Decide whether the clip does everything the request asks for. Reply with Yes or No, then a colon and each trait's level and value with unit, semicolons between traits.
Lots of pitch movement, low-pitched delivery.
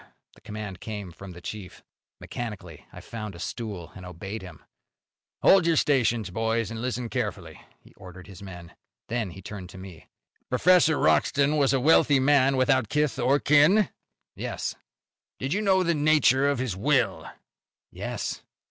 Yes: wide, 6.7 semitones; low, 115 Hz